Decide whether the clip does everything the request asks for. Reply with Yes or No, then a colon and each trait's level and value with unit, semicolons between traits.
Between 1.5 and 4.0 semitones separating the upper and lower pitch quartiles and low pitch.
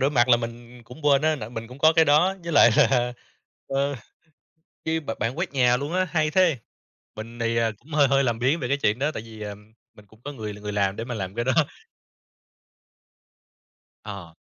No: average, 4.4 semitones; low, 125 Hz